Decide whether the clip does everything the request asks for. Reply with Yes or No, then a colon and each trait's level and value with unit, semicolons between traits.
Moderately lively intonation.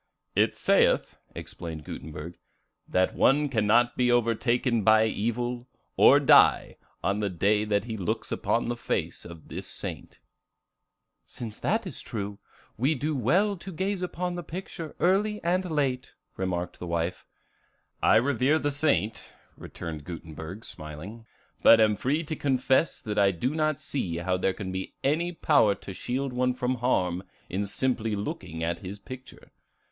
No: wide, 6.6 semitones